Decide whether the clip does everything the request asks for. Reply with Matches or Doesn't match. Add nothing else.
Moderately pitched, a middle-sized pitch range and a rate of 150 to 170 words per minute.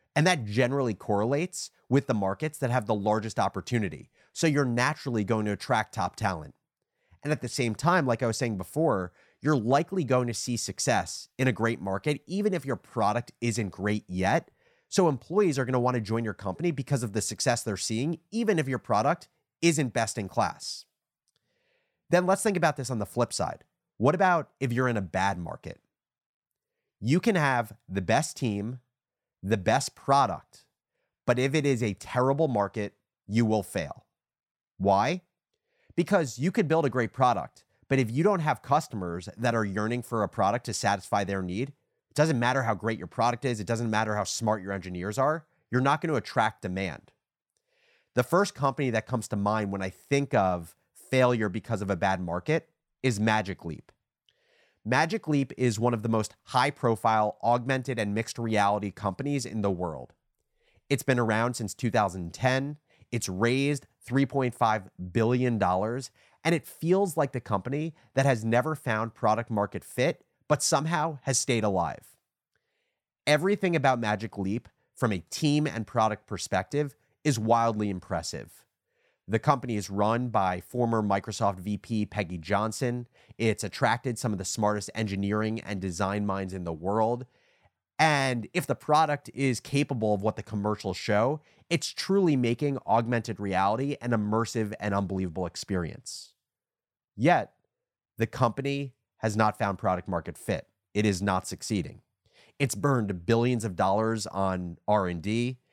Doesn't match